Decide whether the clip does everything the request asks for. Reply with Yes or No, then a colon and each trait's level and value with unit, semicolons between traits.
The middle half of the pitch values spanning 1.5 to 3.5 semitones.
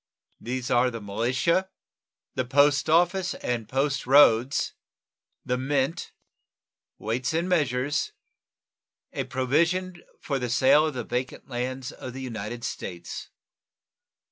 Yes: average, 3.2 semitones